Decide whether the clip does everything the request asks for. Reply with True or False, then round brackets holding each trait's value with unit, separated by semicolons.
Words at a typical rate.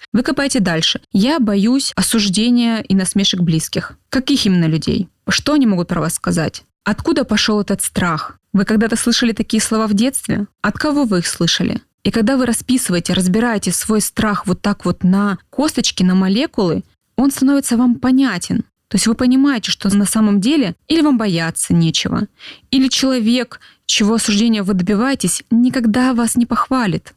False (165 wpm)